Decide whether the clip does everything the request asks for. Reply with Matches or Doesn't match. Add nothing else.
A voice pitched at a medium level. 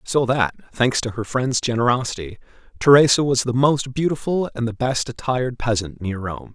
Doesn't match